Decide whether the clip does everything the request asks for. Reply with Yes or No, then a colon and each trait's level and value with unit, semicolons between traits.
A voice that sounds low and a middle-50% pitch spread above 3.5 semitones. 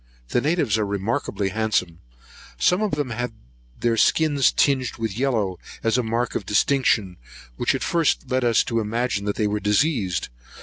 Yes: low, 115 Hz; average, 4.1 semitones